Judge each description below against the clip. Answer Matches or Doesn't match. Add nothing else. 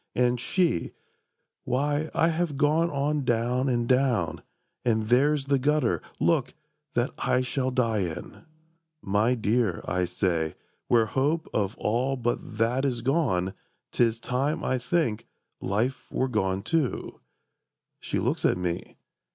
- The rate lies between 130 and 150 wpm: Matches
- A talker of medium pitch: Doesn't match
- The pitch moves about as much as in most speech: Matches